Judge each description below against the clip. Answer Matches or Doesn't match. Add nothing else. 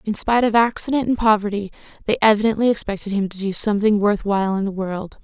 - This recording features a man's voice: Doesn't match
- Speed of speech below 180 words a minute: Doesn't match